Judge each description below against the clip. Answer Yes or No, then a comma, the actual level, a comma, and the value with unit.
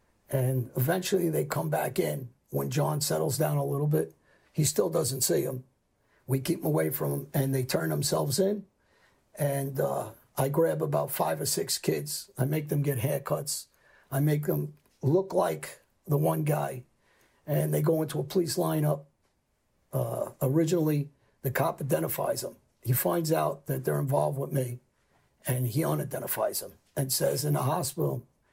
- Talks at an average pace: Yes, average, 170 wpm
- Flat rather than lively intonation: No, average, 3.4 semitones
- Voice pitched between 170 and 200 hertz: No, medium, 140 Hz